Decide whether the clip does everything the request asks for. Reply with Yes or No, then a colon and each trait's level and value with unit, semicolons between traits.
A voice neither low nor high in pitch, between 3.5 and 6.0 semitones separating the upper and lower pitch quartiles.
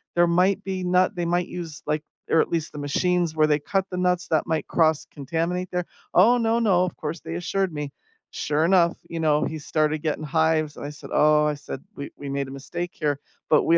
No: medium, 160 Hz; average, 2.9 semitones